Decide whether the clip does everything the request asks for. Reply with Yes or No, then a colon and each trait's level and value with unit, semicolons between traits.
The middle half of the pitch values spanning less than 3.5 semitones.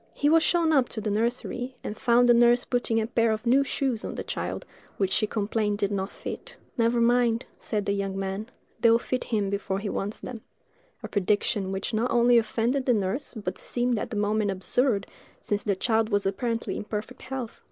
Yes: average, 3.1 semitones